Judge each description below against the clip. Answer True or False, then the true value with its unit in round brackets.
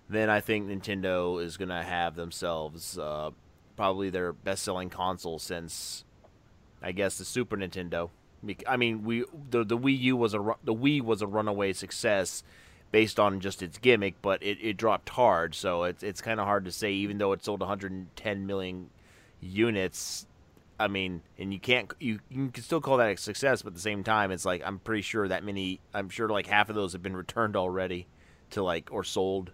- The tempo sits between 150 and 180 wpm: False (200 wpm)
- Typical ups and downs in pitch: True (3.0 semitones)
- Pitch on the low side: True (95 Hz)